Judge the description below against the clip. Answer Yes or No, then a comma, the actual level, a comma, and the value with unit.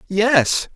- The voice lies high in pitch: Yes, high, 205 Hz